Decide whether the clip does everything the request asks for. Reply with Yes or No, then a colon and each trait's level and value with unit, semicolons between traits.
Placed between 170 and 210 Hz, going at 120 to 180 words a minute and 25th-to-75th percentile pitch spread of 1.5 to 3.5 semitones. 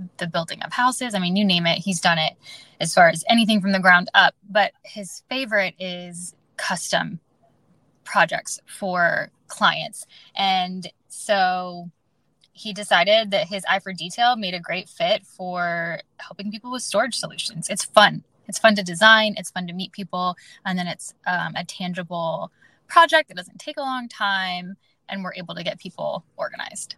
Yes: high, 190 Hz; average, 175 wpm; average, 3.0 semitones